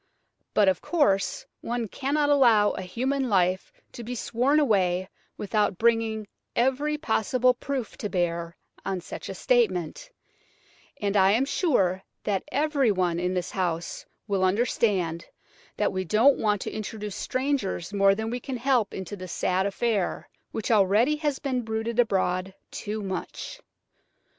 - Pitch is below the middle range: No, high, 215 Hz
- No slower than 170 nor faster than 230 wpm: No, average, 145 wpm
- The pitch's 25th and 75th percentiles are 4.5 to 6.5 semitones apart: Yes, average, 5.1 semitones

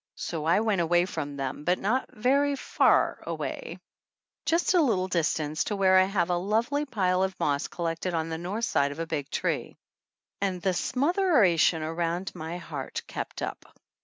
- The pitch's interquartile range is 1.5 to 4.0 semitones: No, average, 4.8 semitones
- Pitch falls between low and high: Yes, medium, 180 Hz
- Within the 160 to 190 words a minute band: Yes, average, 175 wpm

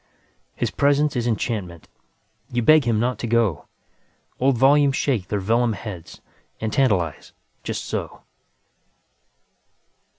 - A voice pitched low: Yes, low, 115 Hz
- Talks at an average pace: No, slow, 100 wpm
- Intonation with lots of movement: No, average, 4.3 semitones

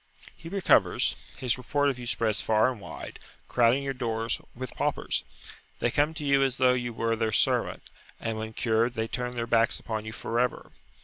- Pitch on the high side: No, low, 120 Hz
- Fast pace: No, average, 195 wpm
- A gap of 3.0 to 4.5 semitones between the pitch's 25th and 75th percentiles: No, narrow, 2.5 semitones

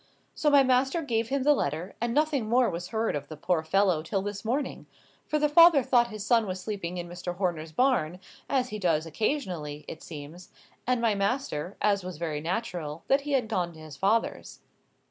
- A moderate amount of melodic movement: No, wide, 6.9 semitones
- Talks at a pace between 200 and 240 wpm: Yes, fast, 205 wpm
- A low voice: No, high, 200 Hz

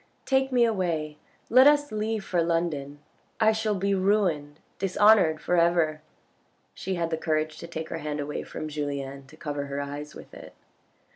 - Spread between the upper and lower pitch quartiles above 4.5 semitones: Yes, average, 5.2 semitones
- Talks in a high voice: No, medium, 165 Hz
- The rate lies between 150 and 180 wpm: Yes, average, 170 wpm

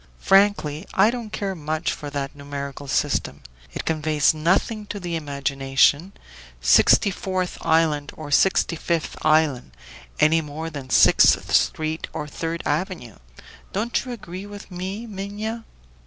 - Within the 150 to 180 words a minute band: No, slow, 135 wpm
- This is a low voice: No, medium, 160 Hz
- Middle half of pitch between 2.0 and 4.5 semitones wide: No, average, 4.9 semitones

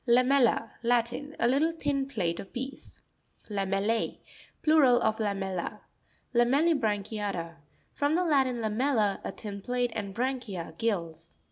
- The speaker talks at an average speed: No, slow, 125 wpm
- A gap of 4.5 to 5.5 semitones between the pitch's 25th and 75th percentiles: Yes, average, 5.1 semitones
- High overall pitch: Yes, high, 235 Hz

